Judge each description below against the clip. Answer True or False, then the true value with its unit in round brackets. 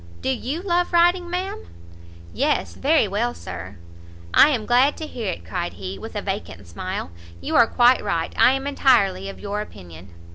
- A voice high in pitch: True (225 Hz)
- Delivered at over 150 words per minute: True (180 wpm)